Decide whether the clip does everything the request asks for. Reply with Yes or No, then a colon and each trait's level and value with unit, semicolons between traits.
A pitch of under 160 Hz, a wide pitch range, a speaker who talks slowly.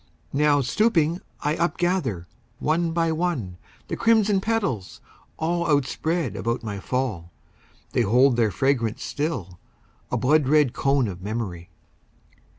Yes: medium, 140 Hz; wide, 7.1 semitones; slow, 125 wpm